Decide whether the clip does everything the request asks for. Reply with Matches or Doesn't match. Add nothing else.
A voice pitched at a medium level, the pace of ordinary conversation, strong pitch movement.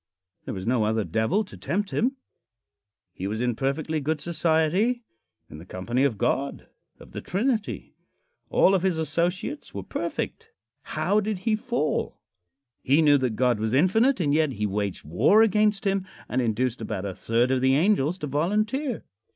Matches